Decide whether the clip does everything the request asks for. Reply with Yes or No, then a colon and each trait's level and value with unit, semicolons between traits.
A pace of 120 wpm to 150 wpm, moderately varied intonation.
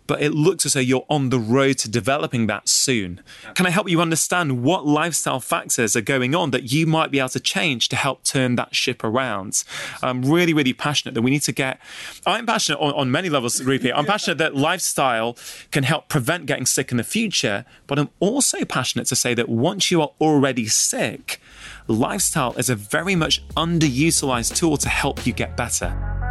No: fast, 205 wpm; average, 4.2 semitones